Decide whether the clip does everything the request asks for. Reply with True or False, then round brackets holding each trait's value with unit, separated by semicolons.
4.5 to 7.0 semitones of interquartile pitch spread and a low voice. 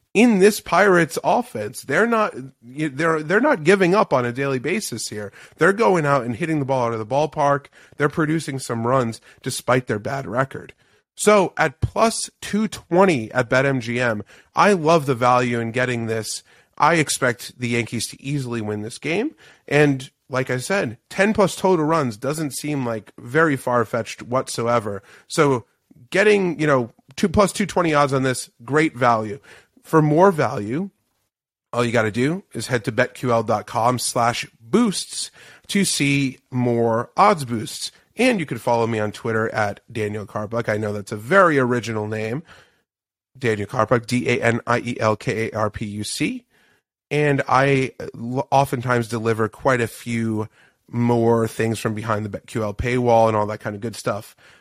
True (5.1 semitones; 125 Hz)